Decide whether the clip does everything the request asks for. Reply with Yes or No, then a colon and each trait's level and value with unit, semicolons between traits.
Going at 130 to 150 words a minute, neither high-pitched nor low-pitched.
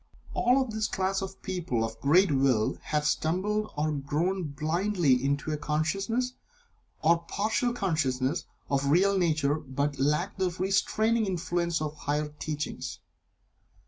Yes: average, 145 wpm; medium, 165 Hz